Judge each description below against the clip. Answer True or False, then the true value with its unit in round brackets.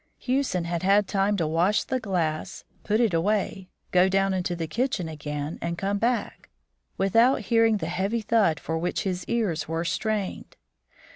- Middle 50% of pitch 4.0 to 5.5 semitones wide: True (4.3 semitones)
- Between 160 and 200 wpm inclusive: True (165 wpm)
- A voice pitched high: True (195 Hz)